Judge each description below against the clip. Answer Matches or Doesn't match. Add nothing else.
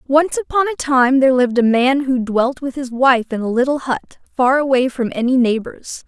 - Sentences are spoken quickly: Matches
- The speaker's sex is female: Matches